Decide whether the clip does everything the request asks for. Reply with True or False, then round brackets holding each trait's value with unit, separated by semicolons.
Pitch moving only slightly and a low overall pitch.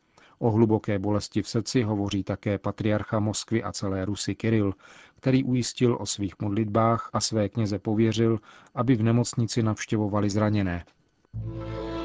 True (2.0 semitones; 110 Hz)